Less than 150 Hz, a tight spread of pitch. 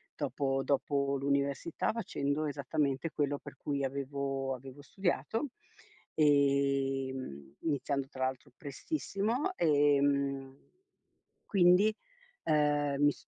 Yes: medium, 140 Hz; narrow, 1.6 semitones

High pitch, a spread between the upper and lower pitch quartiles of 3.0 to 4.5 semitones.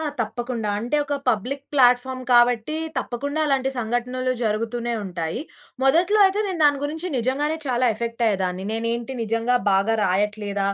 Yes: high, 240 Hz; average, 3.5 semitones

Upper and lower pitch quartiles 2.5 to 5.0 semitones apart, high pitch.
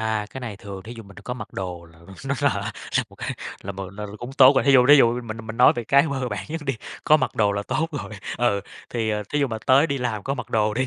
No: average, 4.3 semitones; low, 120 Hz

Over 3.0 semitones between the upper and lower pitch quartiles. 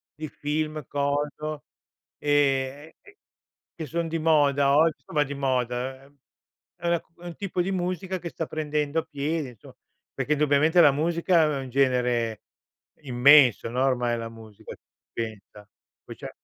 Yes: average, 3.5 semitones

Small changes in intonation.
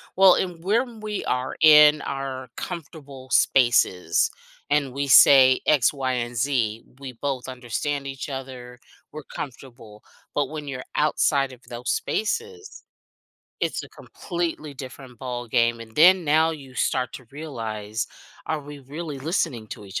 No: average, 3.7 semitones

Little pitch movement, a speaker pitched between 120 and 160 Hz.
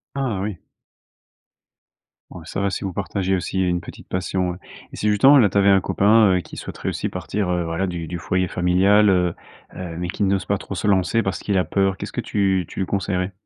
No: narrow, 1.9 semitones; very low, 95 Hz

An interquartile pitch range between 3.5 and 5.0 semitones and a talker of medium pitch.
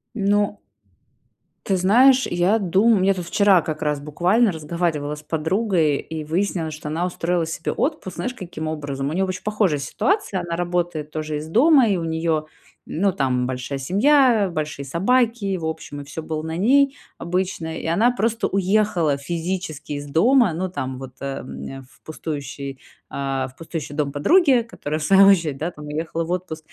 Yes: average, 4.7 semitones; medium, 170 Hz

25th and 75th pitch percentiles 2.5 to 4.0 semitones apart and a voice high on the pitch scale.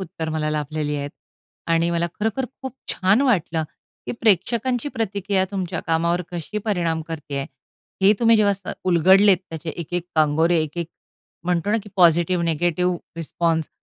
No: average, 3.6 semitones; medium, 175 Hz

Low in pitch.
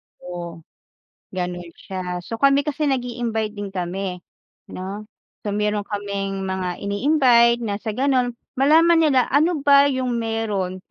No: high, 220 Hz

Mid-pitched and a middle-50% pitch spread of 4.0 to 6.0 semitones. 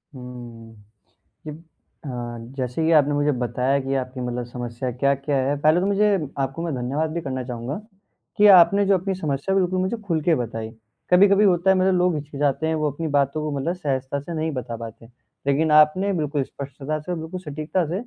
Yes: medium, 150 Hz; average, 4.7 semitones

